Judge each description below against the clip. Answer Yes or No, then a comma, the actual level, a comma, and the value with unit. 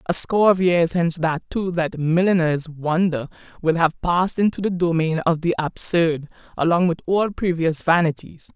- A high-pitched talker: No, medium, 170 Hz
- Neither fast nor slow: Yes, average, 170 wpm